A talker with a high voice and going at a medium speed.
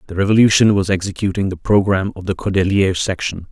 No: very low, 95 Hz; average, 170 wpm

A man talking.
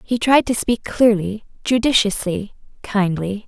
No: female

